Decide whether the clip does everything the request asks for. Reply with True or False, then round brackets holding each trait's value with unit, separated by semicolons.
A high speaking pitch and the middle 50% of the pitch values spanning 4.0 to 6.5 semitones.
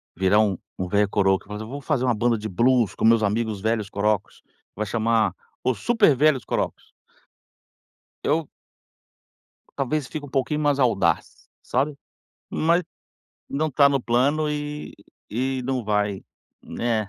False (120 Hz; 5.2 semitones)